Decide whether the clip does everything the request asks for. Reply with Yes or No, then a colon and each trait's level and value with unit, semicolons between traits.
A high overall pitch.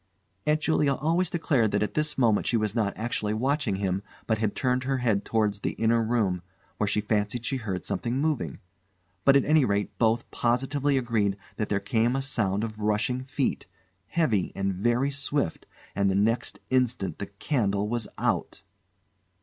No: low, 115 Hz